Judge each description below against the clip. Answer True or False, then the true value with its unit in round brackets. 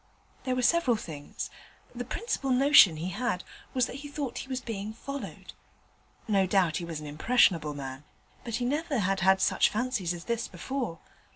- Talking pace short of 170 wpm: False (180 wpm)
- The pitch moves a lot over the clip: True (6.5 semitones)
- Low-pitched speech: False (225 Hz)